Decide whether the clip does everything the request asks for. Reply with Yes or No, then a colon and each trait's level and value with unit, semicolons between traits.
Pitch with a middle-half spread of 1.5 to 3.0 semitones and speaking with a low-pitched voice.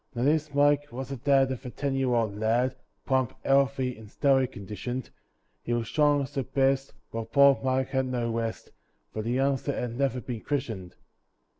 Yes: average, 2.7 semitones; low, 130 Hz